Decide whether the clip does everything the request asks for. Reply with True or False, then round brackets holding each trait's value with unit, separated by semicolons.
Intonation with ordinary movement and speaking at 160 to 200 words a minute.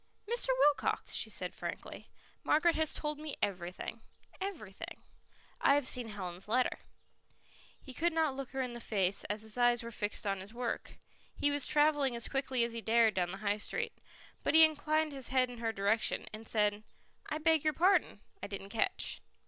False (6.0 semitones; 190 wpm)